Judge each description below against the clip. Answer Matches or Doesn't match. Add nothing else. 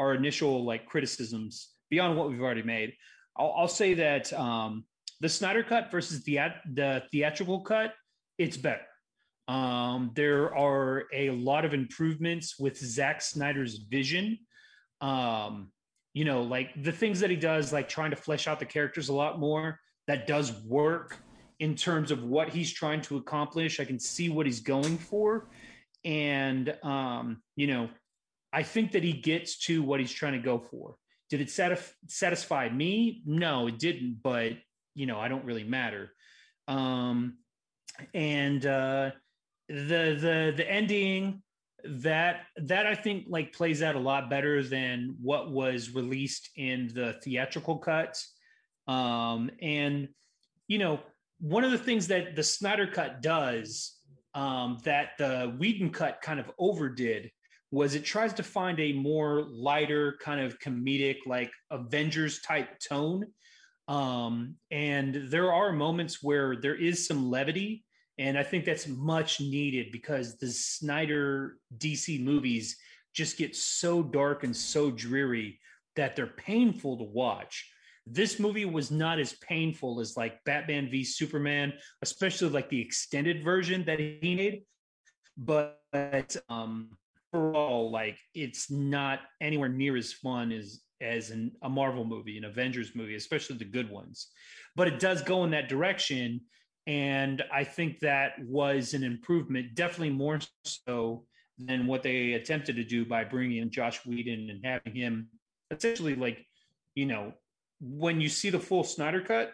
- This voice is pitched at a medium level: Matches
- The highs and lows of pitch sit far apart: Doesn't match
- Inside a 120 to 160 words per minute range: Matches